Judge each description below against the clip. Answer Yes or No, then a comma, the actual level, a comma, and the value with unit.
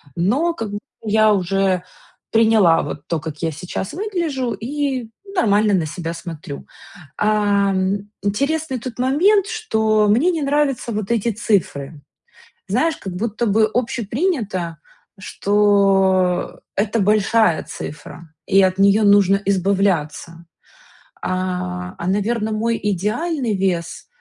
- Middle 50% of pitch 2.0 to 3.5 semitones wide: No, average, 4.0 semitones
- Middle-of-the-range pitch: No, high, 205 Hz